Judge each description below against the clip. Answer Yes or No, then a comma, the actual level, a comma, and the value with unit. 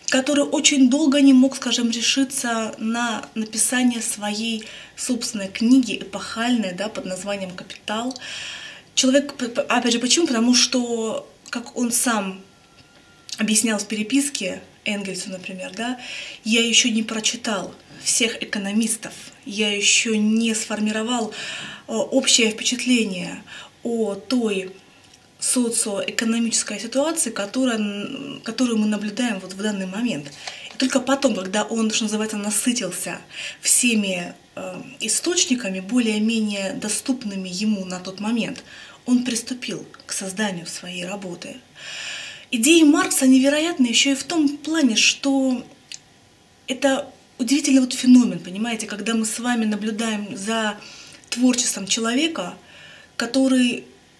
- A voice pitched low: No, high, 230 Hz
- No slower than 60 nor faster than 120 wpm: Yes, average, 115 wpm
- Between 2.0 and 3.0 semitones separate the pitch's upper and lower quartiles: No, average, 3.4 semitones